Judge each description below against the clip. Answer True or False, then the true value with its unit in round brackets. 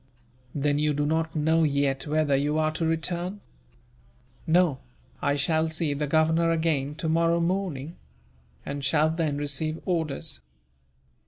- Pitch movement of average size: False (2.2 semitones)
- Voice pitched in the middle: True (155 Hz)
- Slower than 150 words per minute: True (135 wpm)